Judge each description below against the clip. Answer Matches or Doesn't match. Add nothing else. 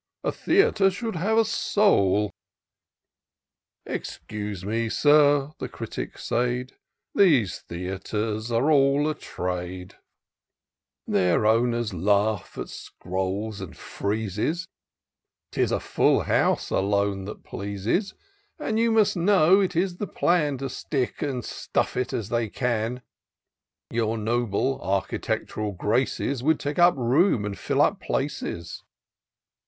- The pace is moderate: Doesn't match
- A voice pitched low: Matches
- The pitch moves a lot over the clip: Matches